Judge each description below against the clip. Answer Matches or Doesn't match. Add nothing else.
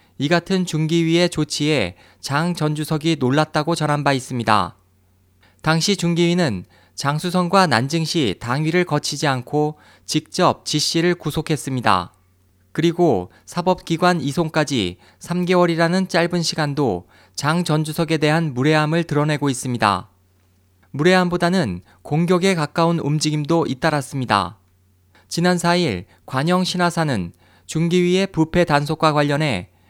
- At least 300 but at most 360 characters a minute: Doesn't match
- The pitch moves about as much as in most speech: Doesn't match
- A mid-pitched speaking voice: Matches